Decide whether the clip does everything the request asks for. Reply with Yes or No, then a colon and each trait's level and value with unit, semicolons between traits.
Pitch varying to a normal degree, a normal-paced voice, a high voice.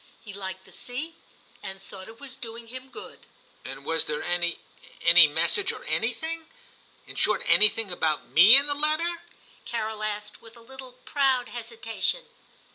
No: wide, 6.0 semitones; average, 175 wpm; high, 225 Hz